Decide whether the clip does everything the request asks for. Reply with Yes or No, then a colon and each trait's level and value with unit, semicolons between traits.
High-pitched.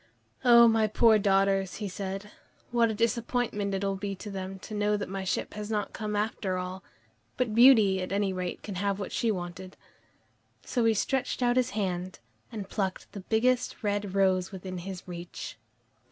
Yes: high, 200 Hz